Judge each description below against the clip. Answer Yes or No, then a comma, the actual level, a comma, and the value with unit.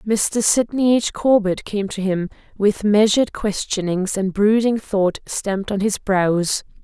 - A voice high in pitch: Yes, high, 205 Hz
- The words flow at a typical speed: Yes, average, 150 wpm